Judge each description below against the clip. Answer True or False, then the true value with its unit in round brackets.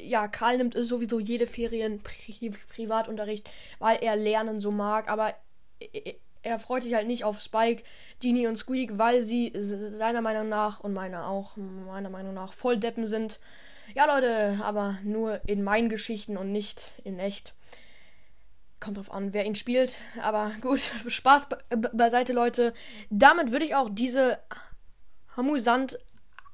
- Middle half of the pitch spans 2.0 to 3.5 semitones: True (2.6 semitones)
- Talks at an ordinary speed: True (165 wpm)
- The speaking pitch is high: True (225 Hz)